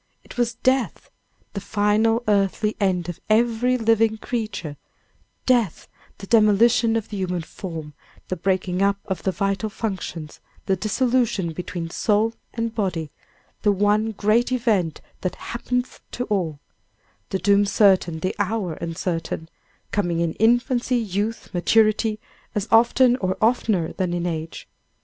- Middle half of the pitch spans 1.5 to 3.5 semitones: No, average, 3.9 semitones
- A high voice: Yes, high, 205 Hz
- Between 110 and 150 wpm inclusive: Yes, slow, 135 wpm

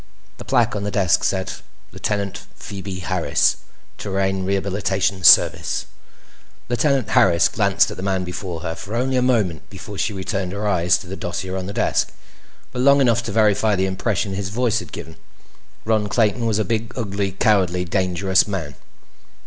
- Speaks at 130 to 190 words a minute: Yes, average, 170 wpm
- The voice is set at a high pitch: No, low, 100 Hz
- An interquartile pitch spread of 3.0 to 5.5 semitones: No, narrow, 2.6 semitones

